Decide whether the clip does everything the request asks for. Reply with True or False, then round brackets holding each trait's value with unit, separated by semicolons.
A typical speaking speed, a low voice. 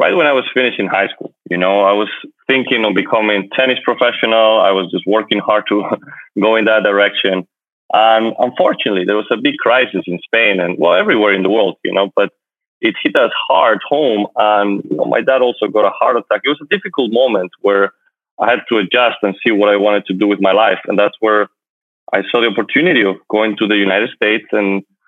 False (225 wpm; 105 Hz)